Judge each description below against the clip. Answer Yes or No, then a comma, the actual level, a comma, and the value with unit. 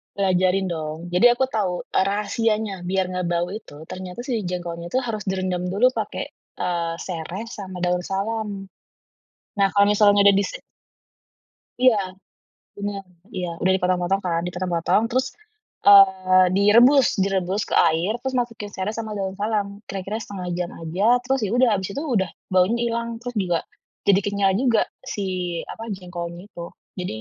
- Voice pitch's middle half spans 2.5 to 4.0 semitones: Yes, average, 2.9 semitones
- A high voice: Yes, high, 195 Hz